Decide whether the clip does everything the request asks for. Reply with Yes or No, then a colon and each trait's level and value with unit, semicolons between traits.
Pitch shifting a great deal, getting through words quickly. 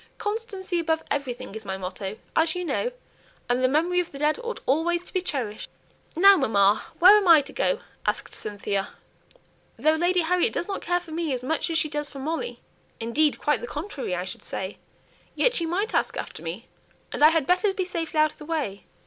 Yes: wide, 5.7 semitones; fast, 210 wpm